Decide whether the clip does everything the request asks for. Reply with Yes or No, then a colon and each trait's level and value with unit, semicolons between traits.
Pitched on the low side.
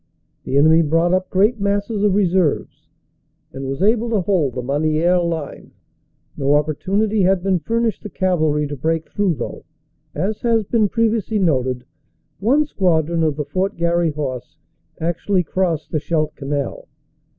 No: medium, 170 Hz